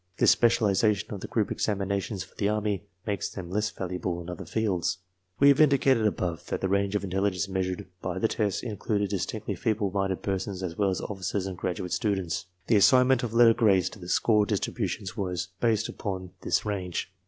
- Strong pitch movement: No, average, 2.7 semitones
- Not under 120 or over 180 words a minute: No, average, 200 wpm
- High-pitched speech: No, low, 100 Hz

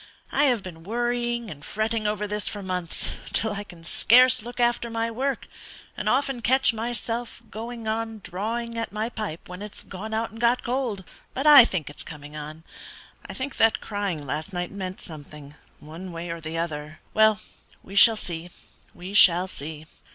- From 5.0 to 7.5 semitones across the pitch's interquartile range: Yes, wide, 5.5 semitones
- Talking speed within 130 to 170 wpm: No, average, 180 wpm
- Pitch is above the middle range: Yes, high, 210 Hz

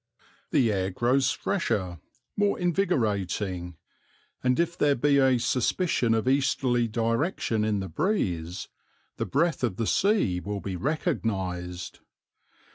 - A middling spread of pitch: No, wide, 7.1 semitones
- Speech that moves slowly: Yes, slow, 120 wpm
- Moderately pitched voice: No, low, 115 Hz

